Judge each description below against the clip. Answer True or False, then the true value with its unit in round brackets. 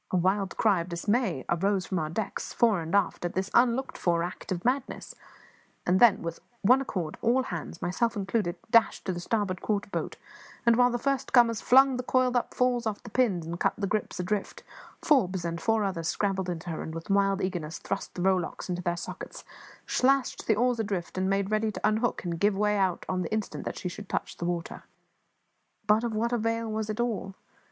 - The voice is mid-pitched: False (200 Hz)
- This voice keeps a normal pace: False (210 wpm)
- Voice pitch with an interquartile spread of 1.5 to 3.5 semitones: False (4.6 semitones)